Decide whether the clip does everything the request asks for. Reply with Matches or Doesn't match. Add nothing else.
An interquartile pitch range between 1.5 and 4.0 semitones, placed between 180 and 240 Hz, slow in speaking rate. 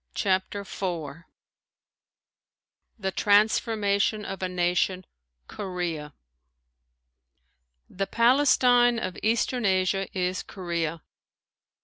Matches